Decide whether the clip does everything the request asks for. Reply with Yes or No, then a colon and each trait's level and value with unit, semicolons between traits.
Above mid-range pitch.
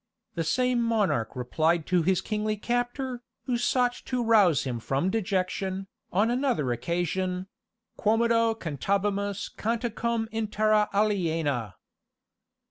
Yes: high, 205 Hz